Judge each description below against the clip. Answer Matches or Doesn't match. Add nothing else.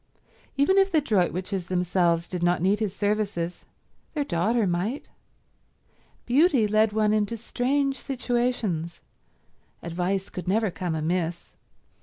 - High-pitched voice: Matches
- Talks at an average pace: Doesn't match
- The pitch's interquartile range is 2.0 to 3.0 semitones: Doesn't match